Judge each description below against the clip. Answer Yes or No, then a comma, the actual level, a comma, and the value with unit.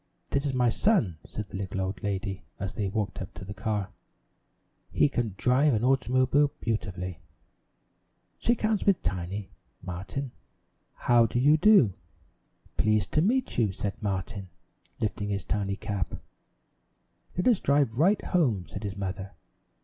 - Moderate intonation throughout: No, wide, 6.0 semitones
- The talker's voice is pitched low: Yes, low, 110 Hz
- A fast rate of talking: No, average, 150 wpm